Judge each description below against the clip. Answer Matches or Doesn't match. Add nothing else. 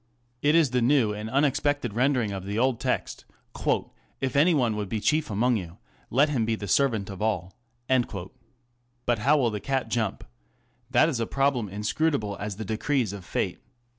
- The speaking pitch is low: Matches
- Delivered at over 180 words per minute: Matches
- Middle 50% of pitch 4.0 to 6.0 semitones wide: Matches